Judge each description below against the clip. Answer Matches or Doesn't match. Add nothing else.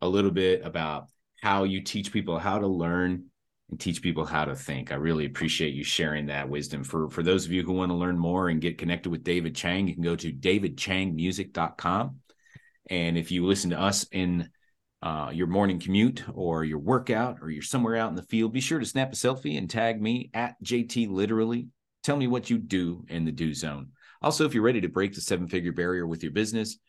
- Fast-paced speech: Matches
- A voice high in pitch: Doesn't match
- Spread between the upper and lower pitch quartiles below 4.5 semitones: Doesn't match